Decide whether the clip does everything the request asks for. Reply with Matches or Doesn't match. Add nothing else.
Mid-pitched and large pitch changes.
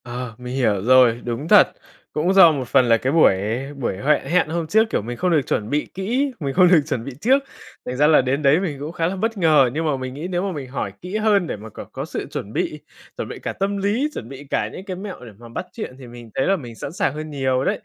Matches